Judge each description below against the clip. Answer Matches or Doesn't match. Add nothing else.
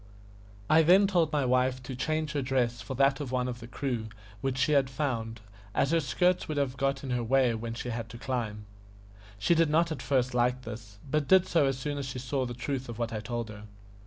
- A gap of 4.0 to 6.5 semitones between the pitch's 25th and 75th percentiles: Doesn't match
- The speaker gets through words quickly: Matches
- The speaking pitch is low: Matches